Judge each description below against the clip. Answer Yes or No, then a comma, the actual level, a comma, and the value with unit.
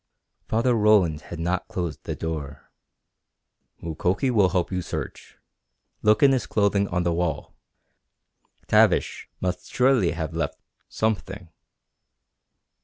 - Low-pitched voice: Yes, very low, 90 Hz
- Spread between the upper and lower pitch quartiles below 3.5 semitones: No, average, 4.1 semitones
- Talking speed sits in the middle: No, slow, 115 wpm